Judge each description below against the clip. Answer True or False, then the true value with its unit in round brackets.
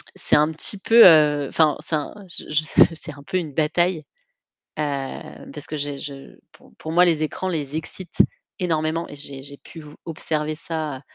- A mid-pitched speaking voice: True (155 Hz)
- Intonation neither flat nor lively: False (2.2 semitones)